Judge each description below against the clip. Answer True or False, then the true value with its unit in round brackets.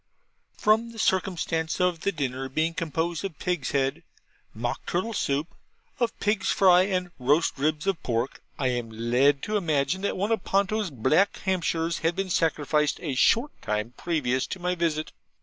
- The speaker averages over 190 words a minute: False (165 wpm)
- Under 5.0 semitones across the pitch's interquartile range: False (5.4 semitones)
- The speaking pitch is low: False (165 Hz)